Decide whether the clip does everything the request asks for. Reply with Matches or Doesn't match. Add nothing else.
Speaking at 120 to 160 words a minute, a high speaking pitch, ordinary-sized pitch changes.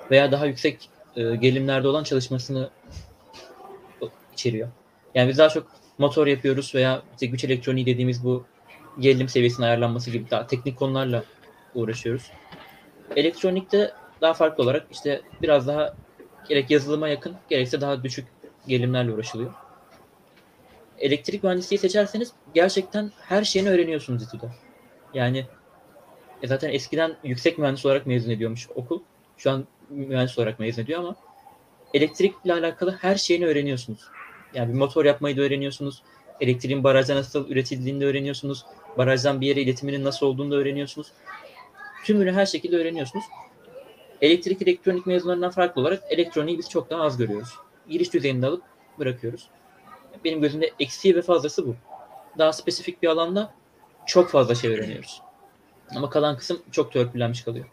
Doesn't match